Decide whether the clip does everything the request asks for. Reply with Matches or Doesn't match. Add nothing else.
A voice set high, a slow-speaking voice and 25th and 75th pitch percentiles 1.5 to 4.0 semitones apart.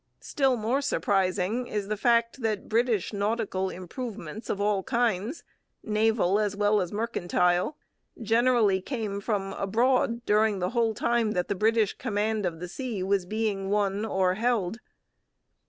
Doesn't match